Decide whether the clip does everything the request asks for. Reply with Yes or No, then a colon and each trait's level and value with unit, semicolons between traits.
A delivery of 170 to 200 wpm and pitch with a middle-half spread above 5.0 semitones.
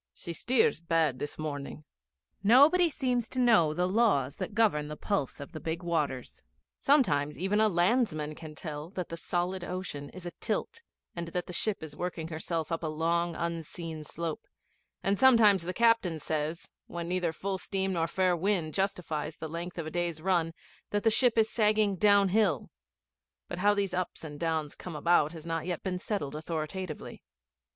No: average, 175 wpm; average, 4.0 semitones